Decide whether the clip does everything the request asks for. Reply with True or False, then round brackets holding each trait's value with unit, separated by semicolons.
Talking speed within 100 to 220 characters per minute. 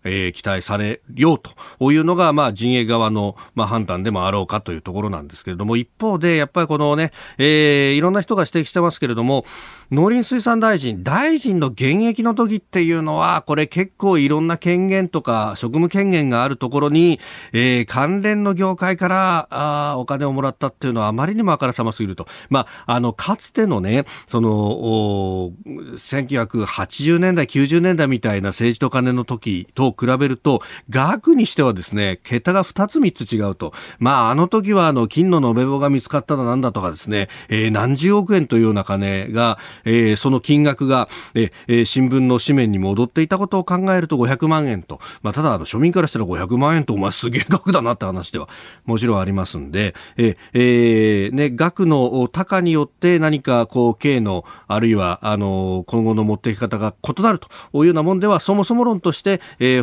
False (365 characters per minute)